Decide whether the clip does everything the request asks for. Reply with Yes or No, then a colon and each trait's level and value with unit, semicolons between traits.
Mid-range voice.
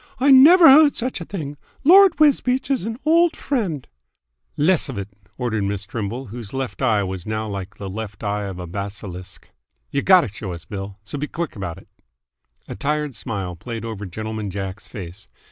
No: low, 110 Hz